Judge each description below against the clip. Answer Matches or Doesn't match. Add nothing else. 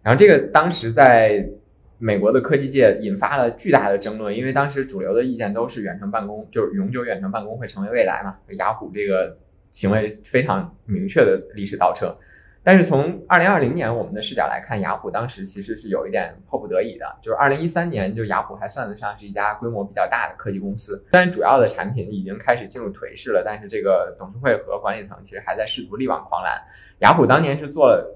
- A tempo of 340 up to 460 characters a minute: Matches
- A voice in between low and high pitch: Doesn't match